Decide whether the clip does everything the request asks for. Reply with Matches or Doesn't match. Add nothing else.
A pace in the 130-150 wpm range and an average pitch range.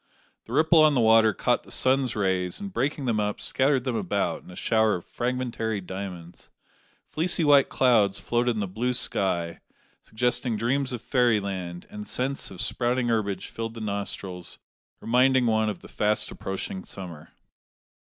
Doesn't match